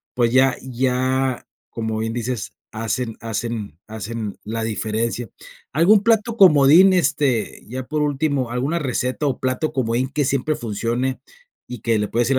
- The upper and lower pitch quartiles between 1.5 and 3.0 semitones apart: No, average, 3.5 semitones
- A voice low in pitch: Yes, low, 125 Hz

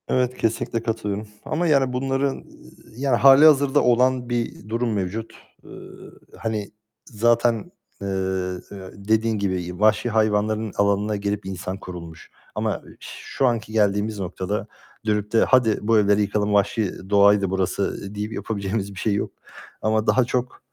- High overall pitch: No, low, 110 Hz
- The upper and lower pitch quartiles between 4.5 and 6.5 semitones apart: No, average, 2.7 semitones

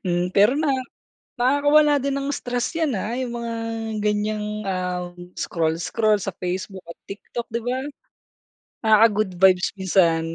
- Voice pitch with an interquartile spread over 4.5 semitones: Yes, average, 5.0 semitones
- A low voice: No, high, 210 Hz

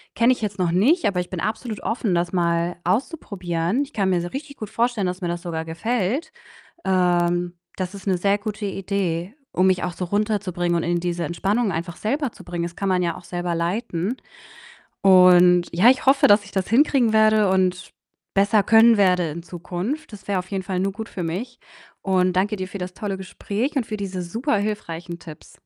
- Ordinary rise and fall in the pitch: Yes, average, 3.5 semitones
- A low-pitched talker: No, high, 190 Hz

